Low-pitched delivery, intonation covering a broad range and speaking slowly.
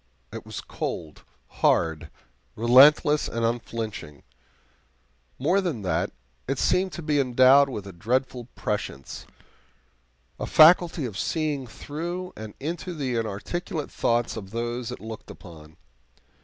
Yes: low, 120 Hz; wide, 5.9 semitones; slow, 125 wpm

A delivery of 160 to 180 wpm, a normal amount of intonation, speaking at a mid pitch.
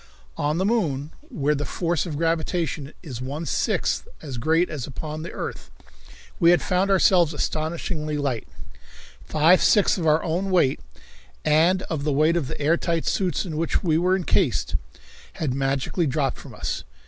Yes: average, 170 wpm; average, 3.1 semitones; medium, 160 Hz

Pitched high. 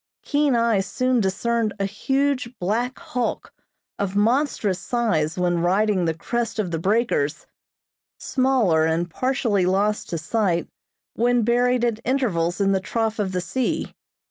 Yes: high, 215 Hz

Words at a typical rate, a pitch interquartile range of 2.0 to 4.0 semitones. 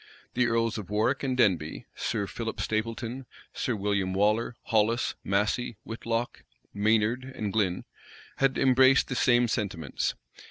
No: slow, 125 wpm; average, 2.9 semitones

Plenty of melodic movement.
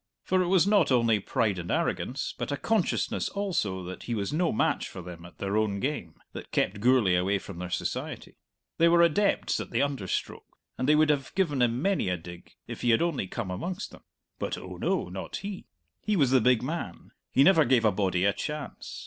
Yes: wide, 8.9 semitones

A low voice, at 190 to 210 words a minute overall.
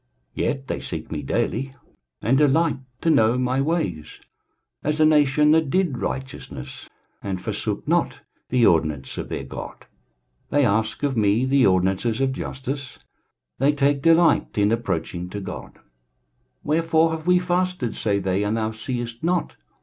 No: low, 130 Hz; average, 155 wpm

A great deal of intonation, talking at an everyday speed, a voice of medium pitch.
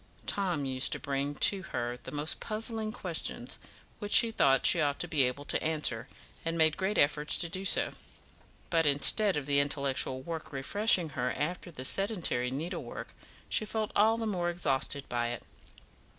Yes: wide, 5.9 semitones; average, 175 wpm; medium, 155 Hz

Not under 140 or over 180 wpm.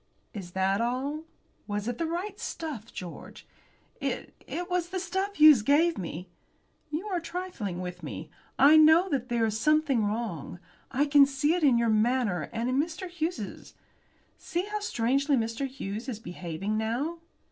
Yes: average, 165 wpm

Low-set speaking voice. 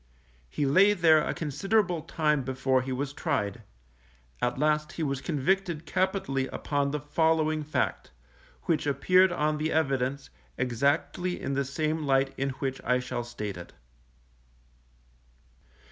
No: medium, 145 Hz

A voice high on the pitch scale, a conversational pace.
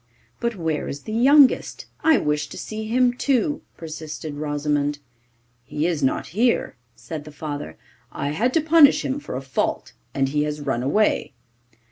No: medium, 155 Hz; average, 165 wpm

